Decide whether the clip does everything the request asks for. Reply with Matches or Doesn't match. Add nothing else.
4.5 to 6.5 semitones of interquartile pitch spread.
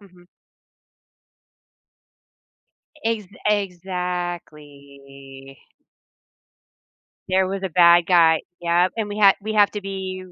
Doesn't match